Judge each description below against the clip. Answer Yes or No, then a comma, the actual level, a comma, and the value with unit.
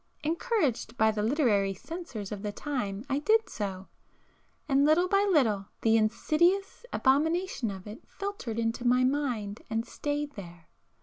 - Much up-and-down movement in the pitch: Yes, wide, 6.7 semitones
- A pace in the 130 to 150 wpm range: Yes, average, 145 wpm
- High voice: Yes, very high, 250 Hz